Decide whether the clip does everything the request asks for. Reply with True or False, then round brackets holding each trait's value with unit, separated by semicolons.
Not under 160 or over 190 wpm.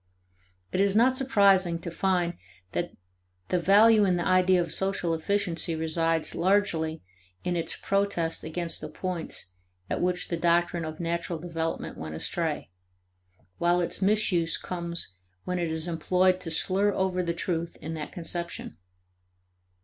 False (145 wpm)